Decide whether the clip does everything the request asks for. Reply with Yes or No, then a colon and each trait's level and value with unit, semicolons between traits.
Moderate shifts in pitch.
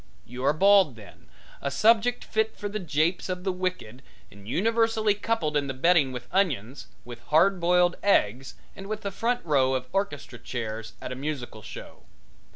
No: wide, 7.6 semitones